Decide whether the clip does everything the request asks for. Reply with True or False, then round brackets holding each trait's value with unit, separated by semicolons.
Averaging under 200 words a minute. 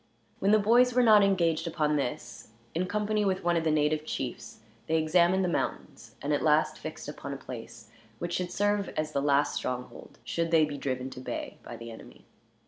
False (205 wpm)